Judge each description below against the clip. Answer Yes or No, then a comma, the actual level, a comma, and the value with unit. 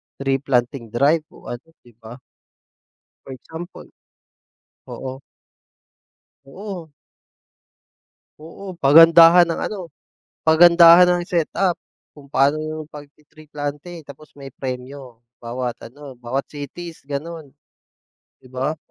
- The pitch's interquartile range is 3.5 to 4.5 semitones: Yes, average, 3.8 semitones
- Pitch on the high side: No, medium, 145 Hz